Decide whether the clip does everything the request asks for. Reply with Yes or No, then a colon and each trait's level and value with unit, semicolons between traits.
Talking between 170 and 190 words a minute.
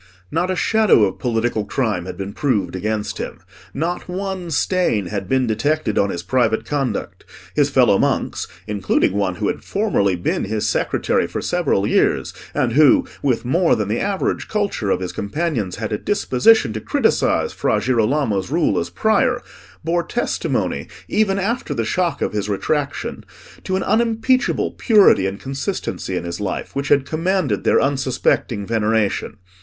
No: average, 160 wpm